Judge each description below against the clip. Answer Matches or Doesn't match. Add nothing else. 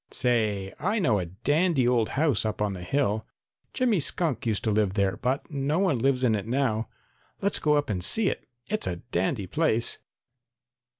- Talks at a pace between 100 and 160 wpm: Doesn't match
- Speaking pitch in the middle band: Doesn't match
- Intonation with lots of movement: Matches